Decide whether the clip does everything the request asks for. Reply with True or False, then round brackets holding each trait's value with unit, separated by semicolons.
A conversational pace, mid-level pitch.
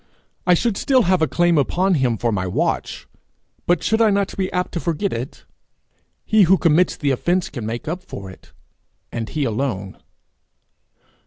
True (175 wpm; 165 Hz)